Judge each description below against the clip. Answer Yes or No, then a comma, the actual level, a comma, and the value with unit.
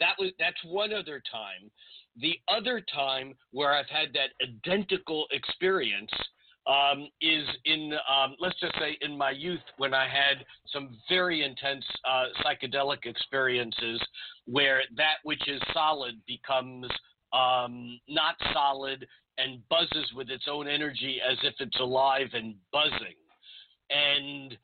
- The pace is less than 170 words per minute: Yes, slow, 135 wpm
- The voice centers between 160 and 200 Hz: No, medium, 140 Hz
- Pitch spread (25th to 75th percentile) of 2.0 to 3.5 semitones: Yes, average, 2.9 semitones